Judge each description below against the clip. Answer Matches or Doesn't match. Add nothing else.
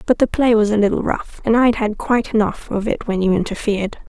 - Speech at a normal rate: Doesn't match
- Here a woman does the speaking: Matches